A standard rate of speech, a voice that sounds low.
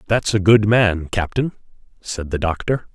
Yes: average, 165 wpm; low, 100 Hz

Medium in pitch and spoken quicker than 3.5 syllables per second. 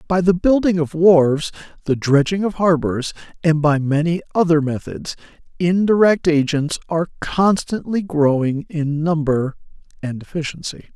Yes: medium, 165 Hz; 4.7 syllables/s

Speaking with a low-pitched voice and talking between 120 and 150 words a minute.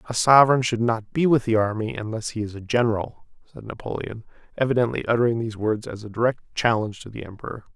No: low, 115 Hz; average, 200 wpm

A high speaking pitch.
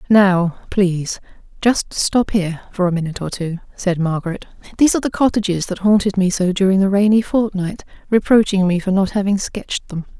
Yes: high, 195 Hz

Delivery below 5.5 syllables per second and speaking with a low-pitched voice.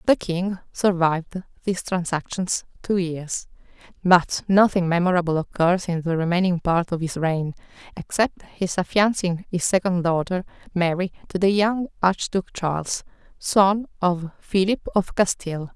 No: 4.6 syllables/s; medium, 180 Hz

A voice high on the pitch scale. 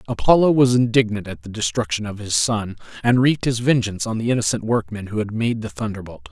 No: low, 115 Hz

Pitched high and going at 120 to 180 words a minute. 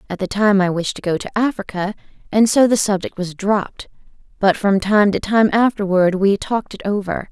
No: high, 200 Hz; fast, 205 wpm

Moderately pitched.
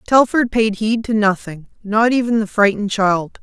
No: high, 215 Hz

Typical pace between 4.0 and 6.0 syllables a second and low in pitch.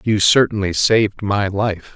Yes: 4.3 syllables/s; low, 100 Hz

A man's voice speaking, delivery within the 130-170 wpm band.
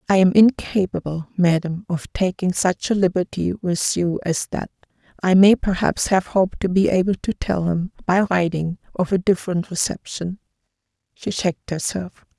No: female; average, 160 wpm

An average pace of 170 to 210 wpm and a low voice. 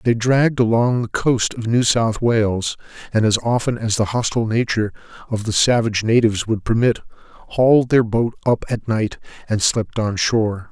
Yes: average, 180 wpm; low, 115 Hz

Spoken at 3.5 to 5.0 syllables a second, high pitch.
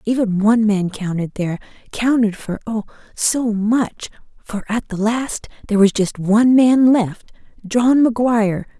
Yes: 4.8 syllables/s; high, 220 Hz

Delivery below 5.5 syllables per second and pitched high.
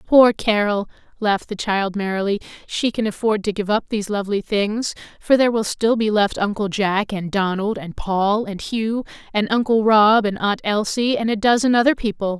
Yes: 5.1 syllables/s; high, 210 Hz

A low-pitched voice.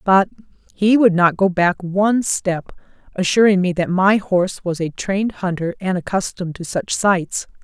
No: medium, 185 Hz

